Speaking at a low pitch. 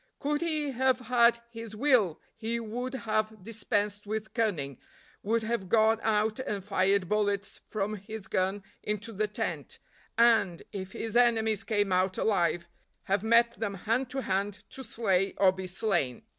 No: high, 215 Hz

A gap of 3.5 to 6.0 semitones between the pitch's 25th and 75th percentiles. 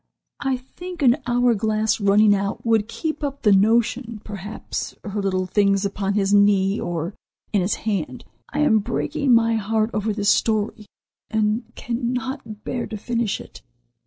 No: average, 2.8 semitones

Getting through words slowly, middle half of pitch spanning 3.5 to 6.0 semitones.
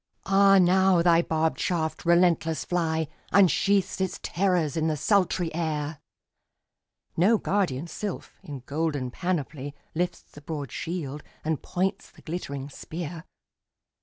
No: slow, 125 wpm; average, 3.0 semitones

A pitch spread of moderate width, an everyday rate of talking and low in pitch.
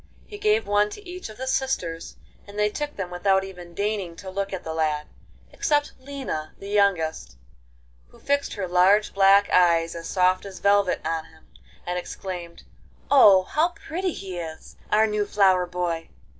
No: average, 3.3 semitones; average, 170 wpm; high, 195 Hz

